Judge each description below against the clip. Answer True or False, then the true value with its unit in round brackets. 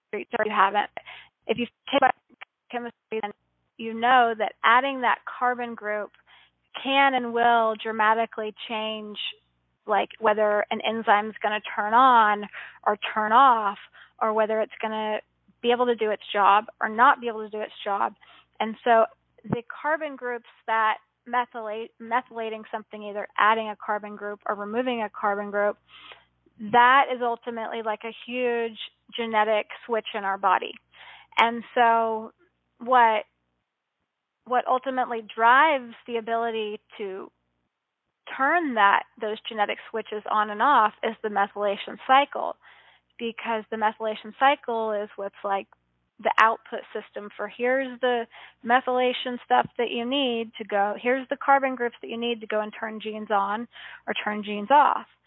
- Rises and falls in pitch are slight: True (2.3 semitones)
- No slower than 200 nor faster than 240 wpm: False (150 wpm)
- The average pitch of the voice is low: False (225 Hz)